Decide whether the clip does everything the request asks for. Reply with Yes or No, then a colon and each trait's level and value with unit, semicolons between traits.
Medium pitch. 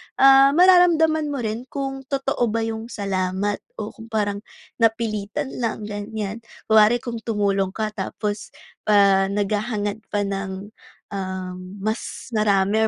No: high, 215 Hz